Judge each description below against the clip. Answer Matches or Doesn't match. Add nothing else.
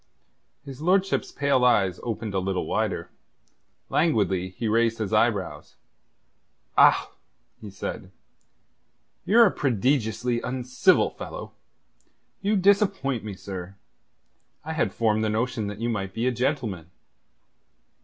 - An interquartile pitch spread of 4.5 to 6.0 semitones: Matches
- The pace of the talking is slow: Matches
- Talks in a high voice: Doesn't match